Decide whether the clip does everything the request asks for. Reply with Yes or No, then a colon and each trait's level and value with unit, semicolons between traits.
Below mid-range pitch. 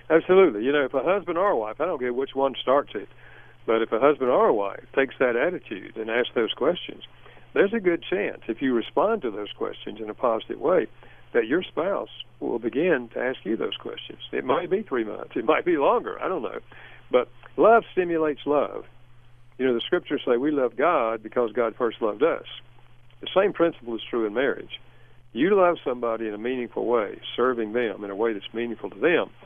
Yes: low, 125 Hz